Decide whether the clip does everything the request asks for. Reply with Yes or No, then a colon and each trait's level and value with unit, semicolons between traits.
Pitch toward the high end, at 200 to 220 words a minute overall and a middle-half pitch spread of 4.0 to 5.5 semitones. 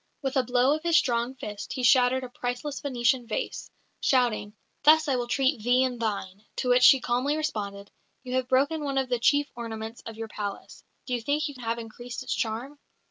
No: very high, 250 Hz; fast, 205 wpm; average, 2.9 semitones